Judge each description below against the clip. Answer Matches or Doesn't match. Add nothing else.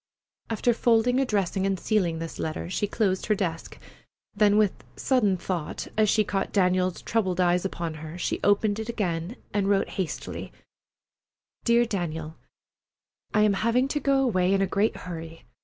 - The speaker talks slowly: Doesn't match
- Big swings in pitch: Doesn't match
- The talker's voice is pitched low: Doesn't match